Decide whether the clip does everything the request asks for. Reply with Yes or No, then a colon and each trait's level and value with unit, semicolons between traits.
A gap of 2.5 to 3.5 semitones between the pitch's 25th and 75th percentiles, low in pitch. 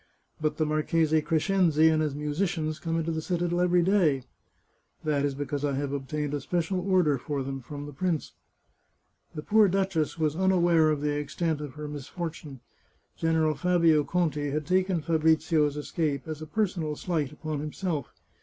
No: average, 2.8 semitones; medium, 155 Hz